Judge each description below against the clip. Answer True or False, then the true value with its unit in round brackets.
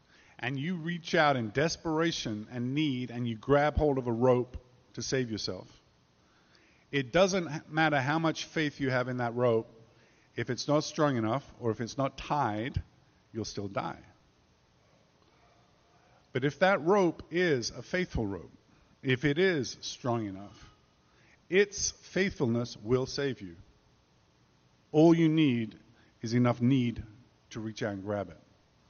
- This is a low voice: True (125 Hz)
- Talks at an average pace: True (150 wpm)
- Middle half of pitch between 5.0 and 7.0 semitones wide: True (5.5 semitones)